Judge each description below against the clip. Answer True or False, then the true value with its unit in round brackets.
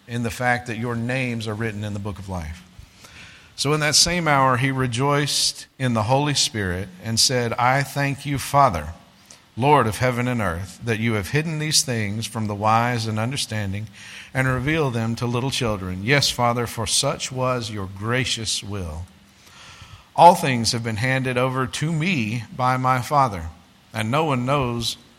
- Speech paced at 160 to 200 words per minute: True (180 wpm)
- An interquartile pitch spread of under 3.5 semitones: False (4.0 semitones)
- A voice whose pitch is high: False (120 Hz)